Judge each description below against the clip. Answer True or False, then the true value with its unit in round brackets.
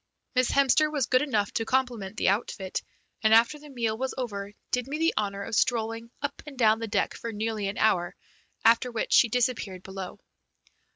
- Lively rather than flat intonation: False (3.6 semitones)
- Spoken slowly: False (190 wpm)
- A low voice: False (230 Hz)